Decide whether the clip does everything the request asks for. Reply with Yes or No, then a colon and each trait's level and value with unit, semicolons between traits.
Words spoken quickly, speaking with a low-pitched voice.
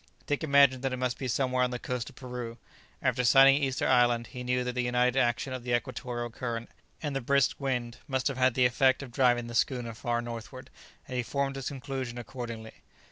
Yes: fast, 215 wpm; low, 125 Hz